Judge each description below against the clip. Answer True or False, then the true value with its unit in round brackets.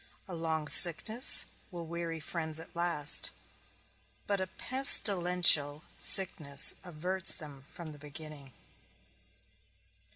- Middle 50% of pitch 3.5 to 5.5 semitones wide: False (2.9 semitones)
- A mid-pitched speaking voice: True (165 Hz)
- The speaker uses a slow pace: True (100 wpm)